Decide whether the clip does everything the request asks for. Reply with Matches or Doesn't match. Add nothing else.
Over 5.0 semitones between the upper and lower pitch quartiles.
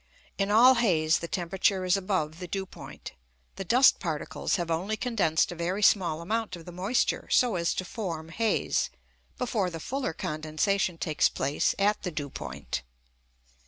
Doesn't match